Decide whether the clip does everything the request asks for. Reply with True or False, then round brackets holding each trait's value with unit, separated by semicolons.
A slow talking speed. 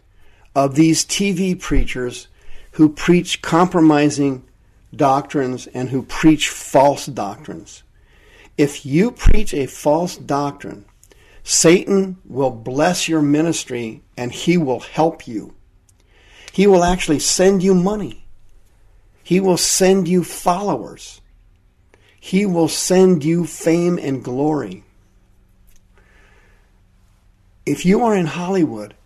True (105 wpm)